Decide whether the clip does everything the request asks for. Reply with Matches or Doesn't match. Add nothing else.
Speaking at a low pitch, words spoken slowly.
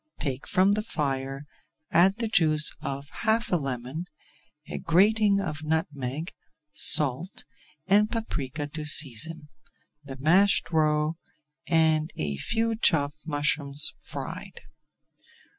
Doesn't match